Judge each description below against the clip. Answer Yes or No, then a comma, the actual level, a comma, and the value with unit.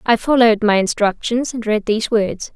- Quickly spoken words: No, average, 190 wpm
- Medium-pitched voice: No, high, 220 Hz